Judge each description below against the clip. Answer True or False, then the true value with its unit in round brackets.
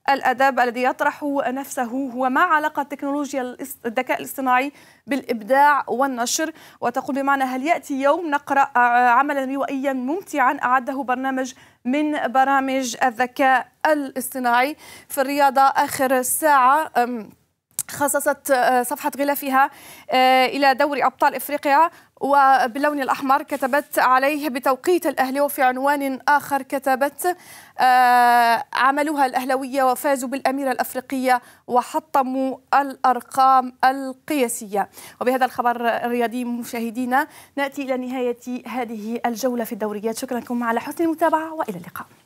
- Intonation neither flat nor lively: False (2.2 semitones)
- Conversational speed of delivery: True (105 wpm)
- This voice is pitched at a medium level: False (265 Hz)